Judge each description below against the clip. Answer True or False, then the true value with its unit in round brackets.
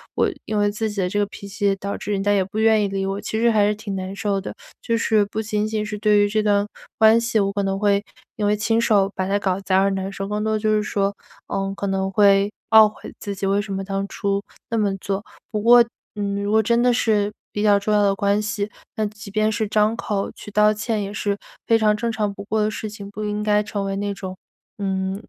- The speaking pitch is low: False (205 Hz)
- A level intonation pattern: True (1.3 semitones)